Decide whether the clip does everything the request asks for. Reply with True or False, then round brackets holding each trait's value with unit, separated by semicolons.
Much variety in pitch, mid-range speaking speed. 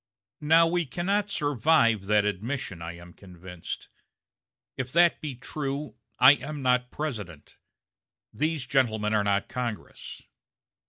False (6.5 semitones; 120 wpm)